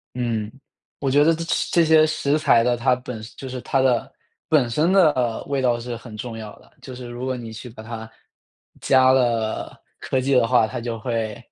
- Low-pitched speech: Yes, low, 125 Hz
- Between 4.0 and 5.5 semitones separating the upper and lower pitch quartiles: No, narrow, 2.5 semitones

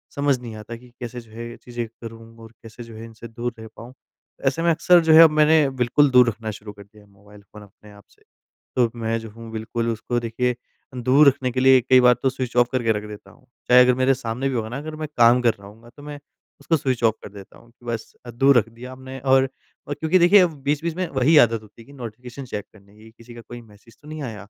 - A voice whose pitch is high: No, low, 120 Hz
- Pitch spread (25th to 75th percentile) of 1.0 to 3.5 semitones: Yes, average, 2.8 semitones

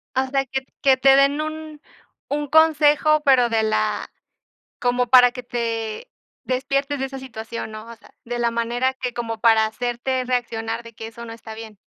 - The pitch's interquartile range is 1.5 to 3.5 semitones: Yes, average, 2.9 semitones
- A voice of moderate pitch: No, high, 245 Hz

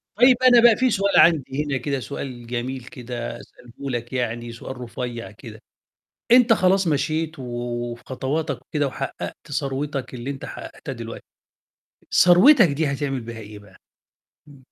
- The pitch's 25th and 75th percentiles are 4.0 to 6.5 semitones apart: Yes, average, 4.8 semitones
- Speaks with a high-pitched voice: No, low, 135 Hz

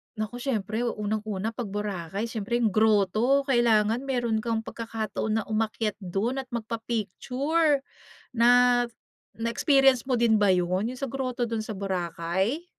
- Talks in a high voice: Yes, high, 225 Hz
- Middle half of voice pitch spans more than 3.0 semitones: No, average, 2.7 semitones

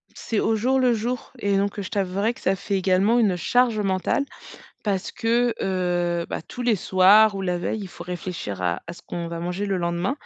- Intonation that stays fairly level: No, average, 3.8 semitones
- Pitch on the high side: Yes, high, 195 Hz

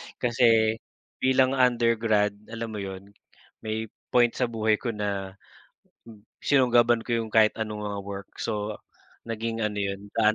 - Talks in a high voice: No, low, 110 Hz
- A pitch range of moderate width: No, narrow, 2.1 semitones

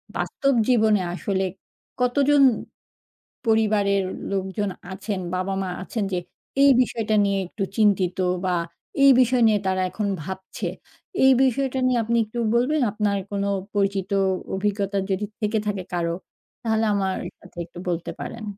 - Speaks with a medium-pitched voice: No, high, 205 Hz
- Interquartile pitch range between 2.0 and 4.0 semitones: Yes, average, 3.2 semitones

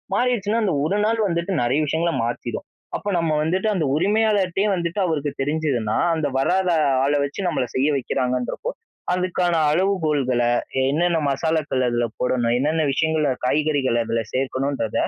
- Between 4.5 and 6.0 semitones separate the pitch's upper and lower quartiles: Yes, average, 5.3 semitones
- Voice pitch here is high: No, medium, 155 Hz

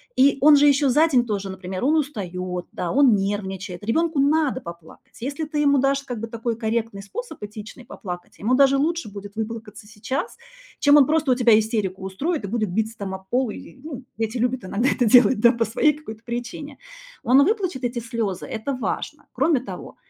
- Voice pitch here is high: Yes, high, 235 Hz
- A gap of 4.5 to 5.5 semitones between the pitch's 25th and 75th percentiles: Yes, average, 5.1 semitones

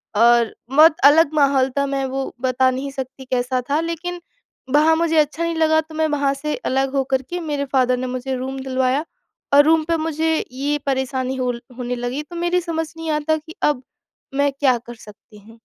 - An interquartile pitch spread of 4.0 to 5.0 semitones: No, average, 3.5 semitones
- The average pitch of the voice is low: No, very high, 280 Hz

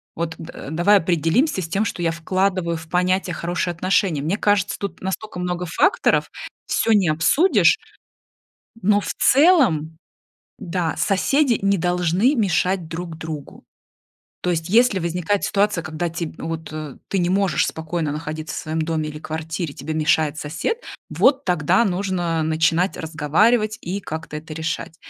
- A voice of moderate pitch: Yes, medium, 175 Hz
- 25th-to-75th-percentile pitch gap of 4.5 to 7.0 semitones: No, average, 3.6 semitones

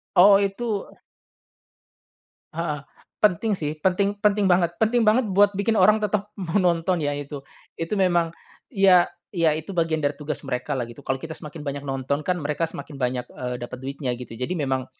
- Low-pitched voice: No, medium, 165 Hz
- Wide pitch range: Yes, wide, 5.7 semitones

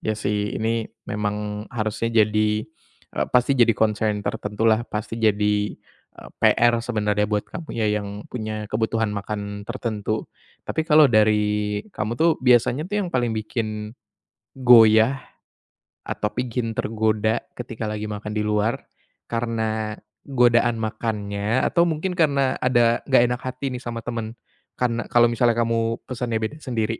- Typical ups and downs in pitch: No, narrow, 2.1 semitones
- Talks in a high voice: No, low, 110 Hz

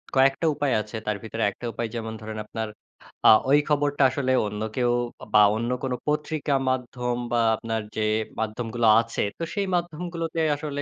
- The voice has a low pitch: Yes, low, 125 Hz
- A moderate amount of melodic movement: Yes, average, 4.6 semitones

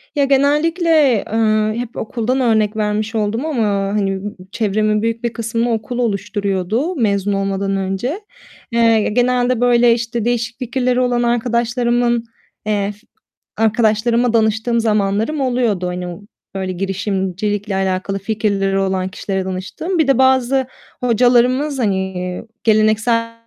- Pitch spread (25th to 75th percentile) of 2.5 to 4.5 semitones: Yes, average, 3.5 semitones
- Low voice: No, high, 225 Hz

